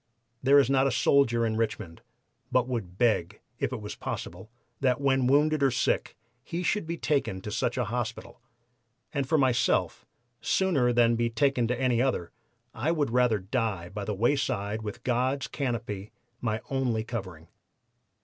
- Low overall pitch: Yes, low, 120 Hz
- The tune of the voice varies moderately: Yes, average, 3.7 semitones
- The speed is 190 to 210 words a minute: No, average, 170 wpm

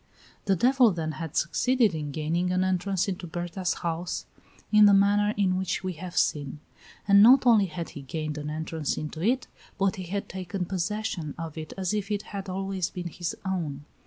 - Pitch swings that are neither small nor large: Yes, average, 3.6 semitones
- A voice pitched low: No, medium, 185 Hz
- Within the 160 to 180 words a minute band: No, average, 190 wpm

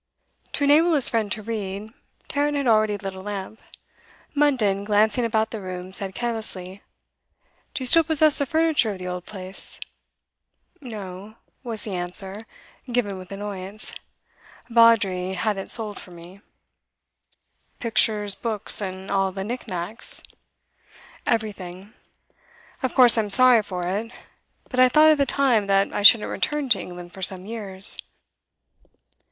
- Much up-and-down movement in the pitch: No, average, 3.8 semitones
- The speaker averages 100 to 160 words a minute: Yes, average, 145 wpm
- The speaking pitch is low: No, high, 210 Hz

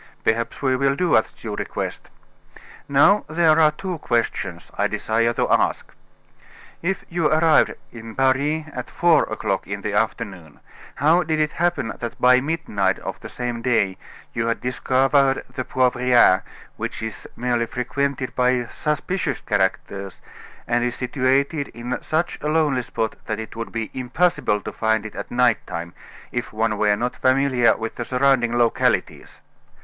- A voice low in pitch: Yes, low, 125 Hz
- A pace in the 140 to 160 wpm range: Yes, average, 155 wpm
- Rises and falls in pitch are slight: No, average, 4.1 semitones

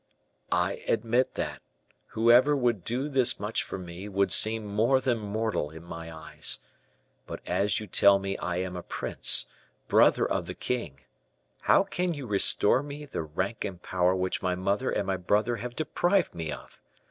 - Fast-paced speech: No, average, 175 wpm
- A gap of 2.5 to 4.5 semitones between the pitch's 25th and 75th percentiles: No, average, 5.0 semitones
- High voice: No, low, 105 Hz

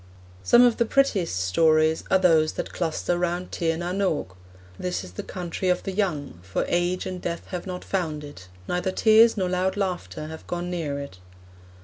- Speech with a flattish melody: No, average, 3.1 semitones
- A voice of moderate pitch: Yes, medium, 175 Hz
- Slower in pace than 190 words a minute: No, average, 195 wpm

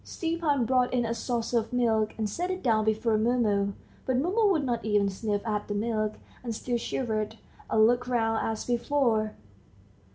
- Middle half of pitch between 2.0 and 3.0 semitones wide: Yes, narrow, 2.5 semitones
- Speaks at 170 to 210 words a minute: Yes, average, 175 wpm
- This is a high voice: Yes, high, 230 Hz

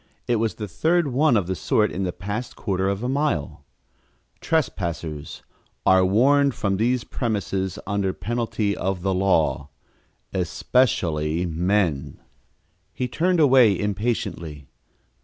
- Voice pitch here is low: Yes, low, 100 Hz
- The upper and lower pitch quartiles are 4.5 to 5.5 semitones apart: Yes, average, 5.2 semitones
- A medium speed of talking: No, slow, 125 wpm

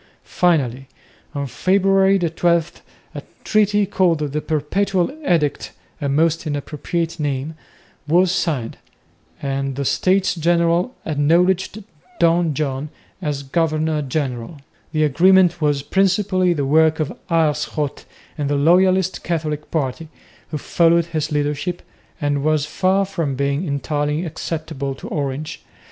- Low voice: No, medium, 160 Hz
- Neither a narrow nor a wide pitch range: Yes, average, 3.3 semitones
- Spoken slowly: Yes, slow, 120 wpm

